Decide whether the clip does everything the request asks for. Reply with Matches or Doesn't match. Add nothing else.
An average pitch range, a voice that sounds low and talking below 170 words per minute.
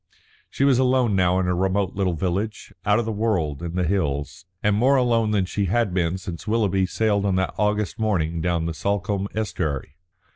Doesn't match